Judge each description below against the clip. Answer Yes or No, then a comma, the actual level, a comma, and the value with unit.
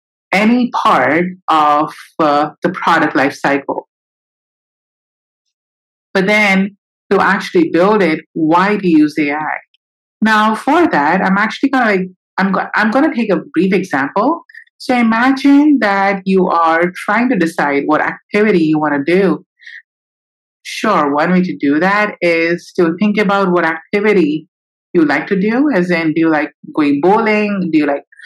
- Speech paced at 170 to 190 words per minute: No, average, 160 wpm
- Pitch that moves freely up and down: No, average, 4.8 semitones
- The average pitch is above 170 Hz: Yes, high, 190 Hz